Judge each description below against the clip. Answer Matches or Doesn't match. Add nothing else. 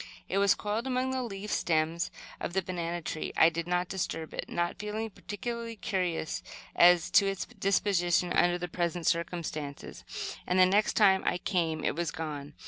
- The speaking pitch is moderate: Matches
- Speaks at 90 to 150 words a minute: Doesn't match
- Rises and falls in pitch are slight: Doesn't match